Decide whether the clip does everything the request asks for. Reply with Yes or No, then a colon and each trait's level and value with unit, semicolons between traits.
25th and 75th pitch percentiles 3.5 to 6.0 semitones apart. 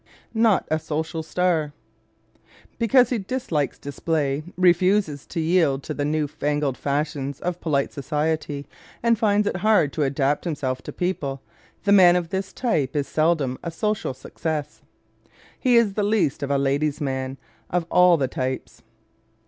Yes: average, 4.5 semitones